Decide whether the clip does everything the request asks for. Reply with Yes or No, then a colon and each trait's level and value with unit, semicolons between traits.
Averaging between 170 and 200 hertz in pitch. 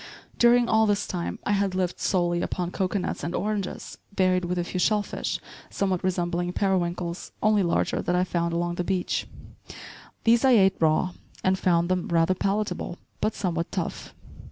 Yes: medium, 185 Hz